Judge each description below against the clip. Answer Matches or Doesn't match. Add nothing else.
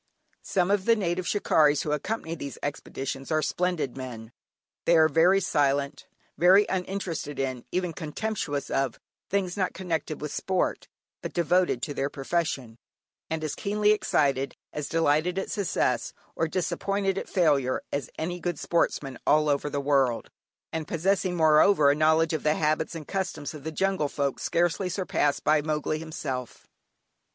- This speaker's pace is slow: Doesn't match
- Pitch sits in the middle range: Matches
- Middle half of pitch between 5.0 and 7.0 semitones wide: Doesn't match